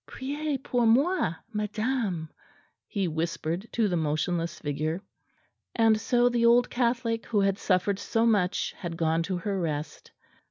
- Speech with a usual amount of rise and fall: No, wide, 5.8 semitones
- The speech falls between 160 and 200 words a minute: No, average, 145 wpm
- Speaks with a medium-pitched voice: No, high, 205 Hz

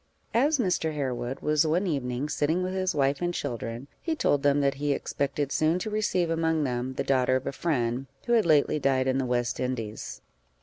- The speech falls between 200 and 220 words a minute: Yes, fast, 205 wpm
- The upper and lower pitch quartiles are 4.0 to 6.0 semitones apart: Yes, average, 4.4 semitones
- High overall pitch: No, medium, 145 Hz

